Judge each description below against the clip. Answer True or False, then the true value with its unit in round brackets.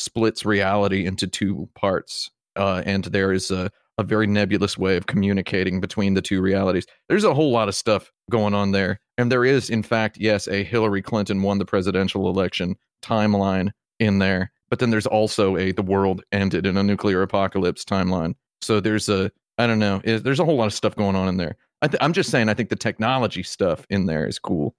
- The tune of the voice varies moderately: False (2.2 semitones)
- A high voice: False (100 Hz)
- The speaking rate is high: True (215 wpm)